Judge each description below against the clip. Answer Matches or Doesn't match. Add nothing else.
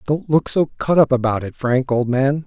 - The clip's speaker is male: Matches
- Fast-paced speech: Matches